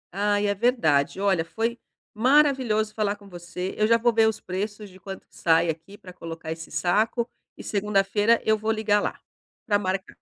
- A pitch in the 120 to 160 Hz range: No, high, 205 Hz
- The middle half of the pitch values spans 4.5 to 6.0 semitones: No, average, 3.0 semitones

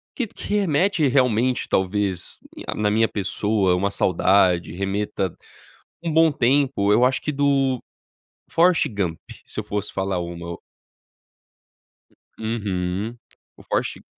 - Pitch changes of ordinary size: No, wide, 6.1 semitones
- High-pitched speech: No, low, 105 Hz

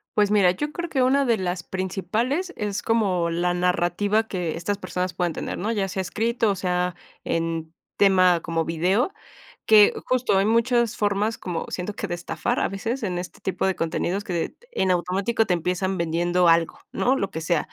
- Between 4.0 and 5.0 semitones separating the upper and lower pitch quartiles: No, average, 3.5 semitones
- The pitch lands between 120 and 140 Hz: No, high, 190 Hz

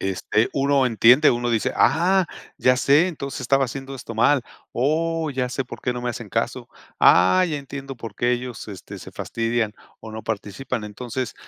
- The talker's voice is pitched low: Yes, low, 125 Hz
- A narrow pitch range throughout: No, average, 3.2 semitones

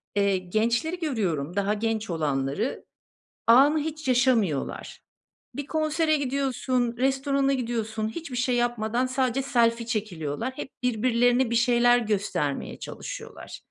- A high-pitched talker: Yes, high, 240 Hz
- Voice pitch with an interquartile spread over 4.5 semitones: No, average, 3.7 semitones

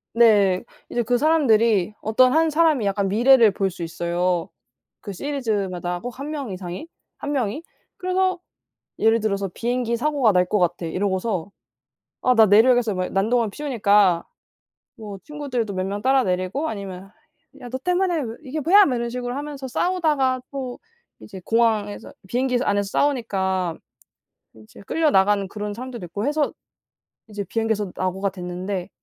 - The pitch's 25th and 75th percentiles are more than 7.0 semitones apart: No, average, 5.3 semitones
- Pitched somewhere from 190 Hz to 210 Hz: No, high, 225 Hz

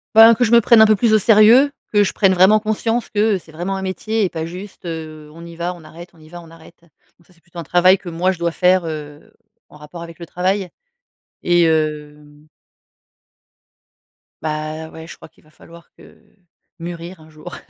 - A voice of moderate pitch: Yes, medium, 175 Hz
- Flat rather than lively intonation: No, average, 3.4 semitones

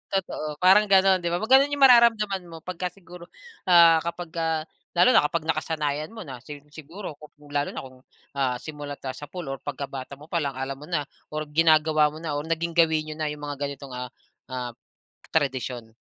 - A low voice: No, medium, 155 Hz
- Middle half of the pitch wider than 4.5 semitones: No, average, 3.3 semitones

